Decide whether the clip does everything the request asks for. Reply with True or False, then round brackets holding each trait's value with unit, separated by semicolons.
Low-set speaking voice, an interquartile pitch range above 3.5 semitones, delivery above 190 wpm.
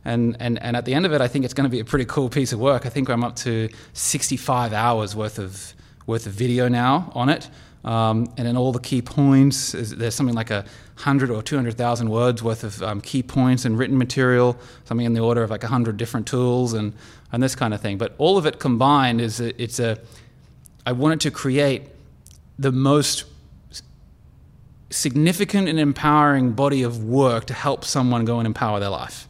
False (125 Hz; 3.0 semitones; 205 wpm)